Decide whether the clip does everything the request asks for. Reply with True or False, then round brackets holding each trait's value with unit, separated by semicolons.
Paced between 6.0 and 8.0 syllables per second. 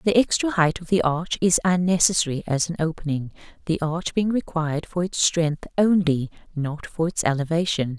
False (5.2 syllables/s)